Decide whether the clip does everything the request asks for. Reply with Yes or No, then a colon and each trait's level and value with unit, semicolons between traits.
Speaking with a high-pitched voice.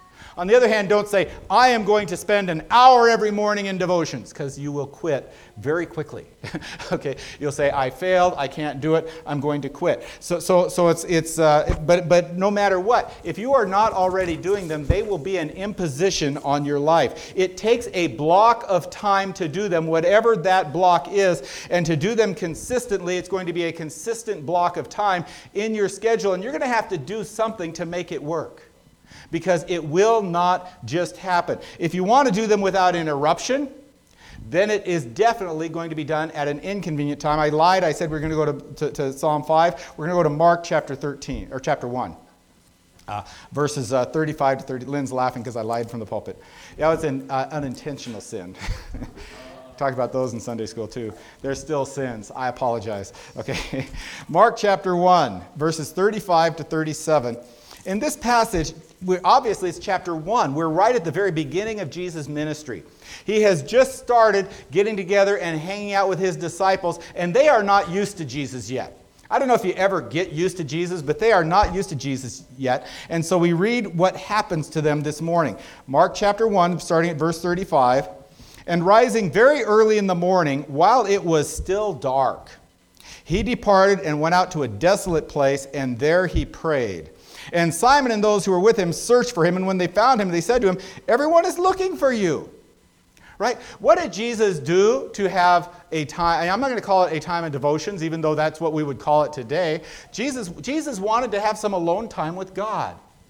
No: medium, 175 Hz